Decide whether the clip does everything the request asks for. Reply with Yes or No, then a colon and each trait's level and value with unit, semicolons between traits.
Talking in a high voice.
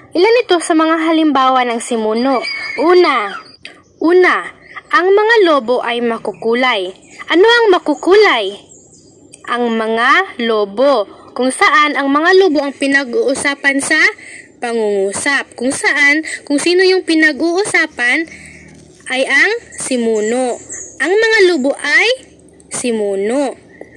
Yes: very high, 300 Hz